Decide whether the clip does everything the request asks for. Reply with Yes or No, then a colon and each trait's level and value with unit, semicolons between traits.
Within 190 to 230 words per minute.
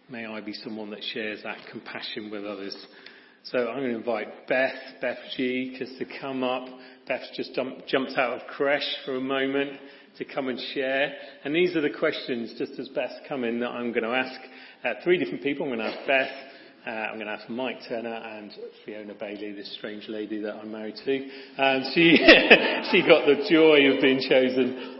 Yes: fast, 205 wpm